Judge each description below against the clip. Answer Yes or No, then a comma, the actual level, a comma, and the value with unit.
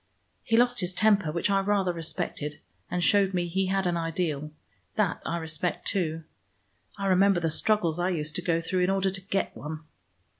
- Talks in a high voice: No, medium, 180 Hz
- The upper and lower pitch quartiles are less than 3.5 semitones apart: Yes, average, 3.0 semitones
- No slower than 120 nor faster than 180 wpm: No, average, 190 wpm